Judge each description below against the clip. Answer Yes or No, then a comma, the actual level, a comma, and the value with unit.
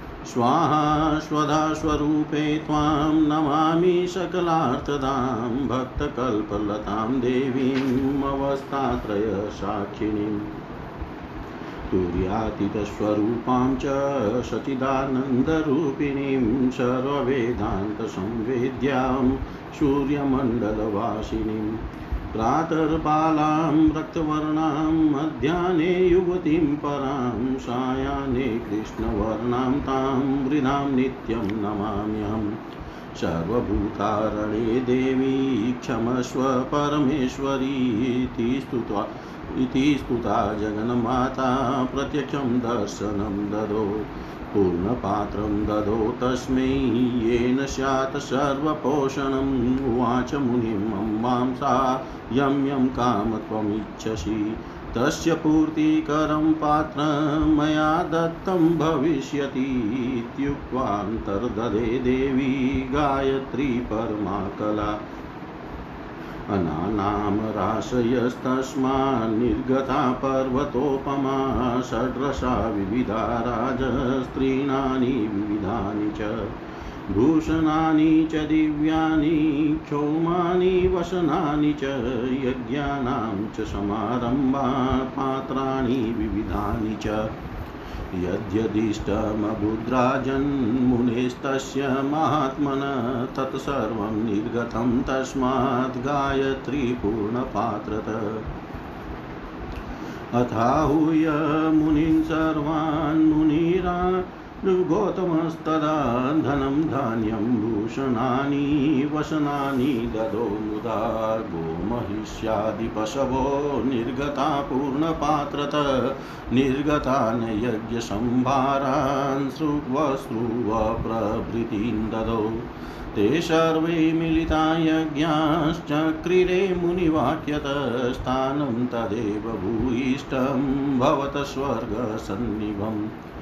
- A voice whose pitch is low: Yes, low, 130 Hz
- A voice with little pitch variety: No, average, 4.7 semitones